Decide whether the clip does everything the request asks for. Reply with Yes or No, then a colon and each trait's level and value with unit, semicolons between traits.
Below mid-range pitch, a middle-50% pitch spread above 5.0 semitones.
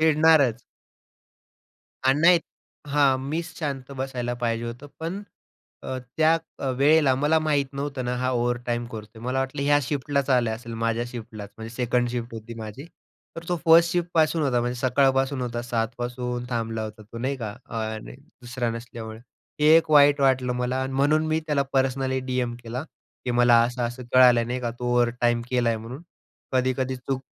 No: low, 125 Hz; average, 2.9 semitones